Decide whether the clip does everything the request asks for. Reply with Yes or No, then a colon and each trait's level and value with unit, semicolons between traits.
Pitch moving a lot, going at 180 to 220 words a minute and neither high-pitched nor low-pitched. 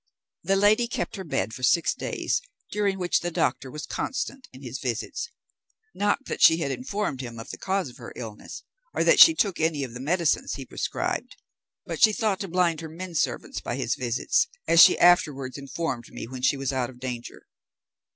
Yes: wide, 6.9 semitones; average, 200 wpm; medium, 155 Hz